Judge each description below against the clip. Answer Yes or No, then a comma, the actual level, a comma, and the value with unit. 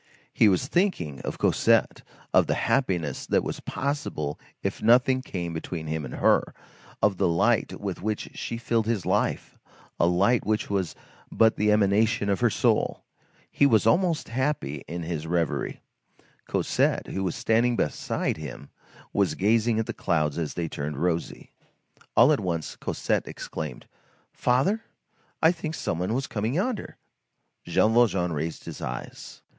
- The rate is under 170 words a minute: Yes, average, 160 wpm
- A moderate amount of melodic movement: No, wide, 6.2 semitones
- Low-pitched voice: Yes, low, 100 Hz